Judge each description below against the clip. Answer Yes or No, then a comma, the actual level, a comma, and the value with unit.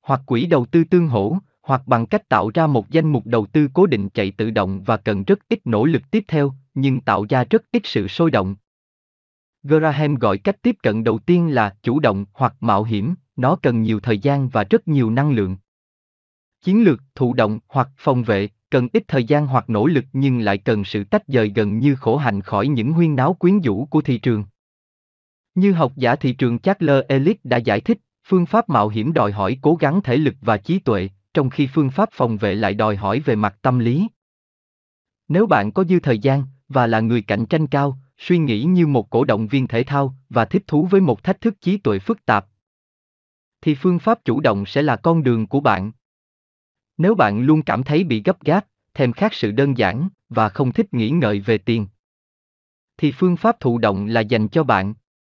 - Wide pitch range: Yes, wide, 6.5 semitones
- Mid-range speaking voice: No, low, 130 Hz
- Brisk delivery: No, average, 220 wpm